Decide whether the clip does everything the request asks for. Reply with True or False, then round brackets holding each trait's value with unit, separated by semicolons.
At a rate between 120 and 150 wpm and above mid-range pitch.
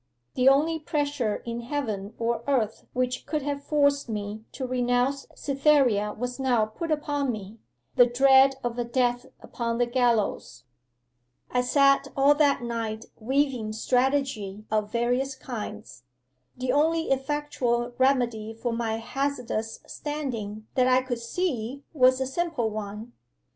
True (140 wpm; 250 Hz)